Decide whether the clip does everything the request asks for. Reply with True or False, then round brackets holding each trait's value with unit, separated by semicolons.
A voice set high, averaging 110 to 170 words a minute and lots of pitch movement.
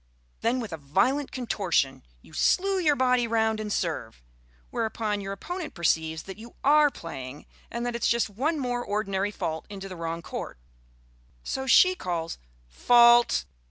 True (215 Hz; 160 wpm; 6.8 semitones)